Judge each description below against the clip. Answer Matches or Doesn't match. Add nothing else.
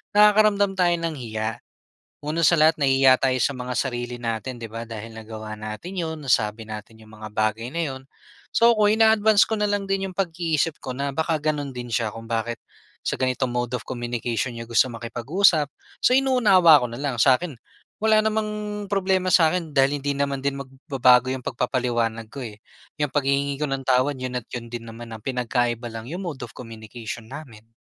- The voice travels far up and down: Matches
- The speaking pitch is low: Matches